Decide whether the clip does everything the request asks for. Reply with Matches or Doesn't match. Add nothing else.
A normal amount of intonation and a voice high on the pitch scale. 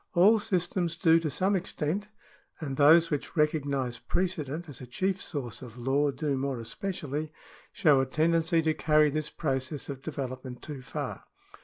Doesn't match